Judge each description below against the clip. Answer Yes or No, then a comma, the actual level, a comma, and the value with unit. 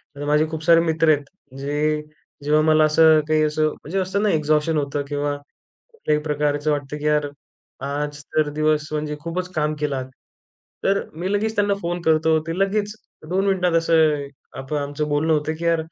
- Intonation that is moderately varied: No, narrow, 2.0 semitones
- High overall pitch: No, medium, 155 Hz